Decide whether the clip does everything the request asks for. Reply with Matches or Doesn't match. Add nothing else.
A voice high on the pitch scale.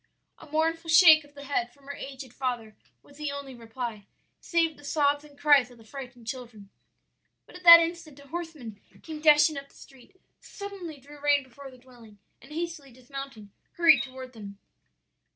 Matches